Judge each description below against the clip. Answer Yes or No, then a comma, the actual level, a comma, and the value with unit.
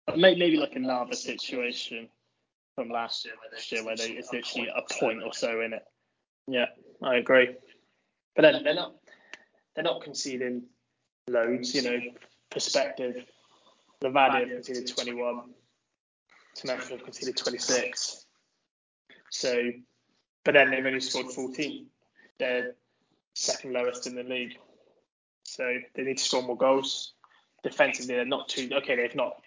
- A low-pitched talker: Yes, low, 125 Hz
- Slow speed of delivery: No, average, 145 wpm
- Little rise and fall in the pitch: Yes, narrow, 1.2 semitones